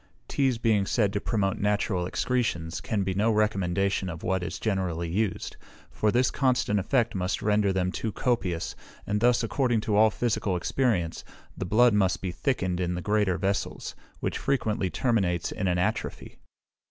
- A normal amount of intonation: Yes, average, 3.7 semitones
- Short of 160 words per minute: No, average, 165 wpm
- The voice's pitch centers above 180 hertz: No, low, 100 Hz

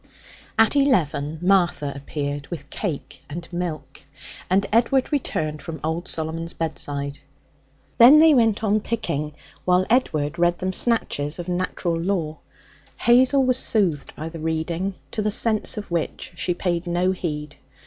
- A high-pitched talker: No, medium, 175 Hz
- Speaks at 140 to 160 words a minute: Yes, average, 145 wpm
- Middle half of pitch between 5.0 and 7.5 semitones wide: Yes, wide, 5.4 semitones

